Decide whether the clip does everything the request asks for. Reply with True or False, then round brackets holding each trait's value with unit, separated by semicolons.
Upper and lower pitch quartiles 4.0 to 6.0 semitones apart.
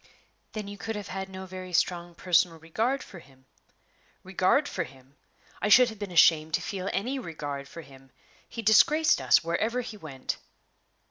True (5.1 semitones)